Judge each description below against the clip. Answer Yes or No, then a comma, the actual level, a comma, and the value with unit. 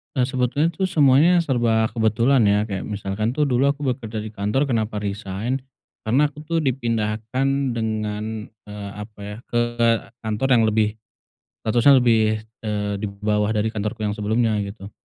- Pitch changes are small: No, average, 3.6 semitones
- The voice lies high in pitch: No, low, 110 Hz